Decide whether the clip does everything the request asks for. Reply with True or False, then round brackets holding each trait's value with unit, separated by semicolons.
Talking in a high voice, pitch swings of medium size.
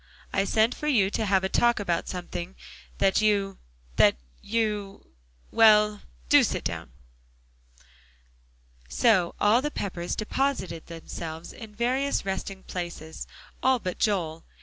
True (200 Hz; 3.7 semitones)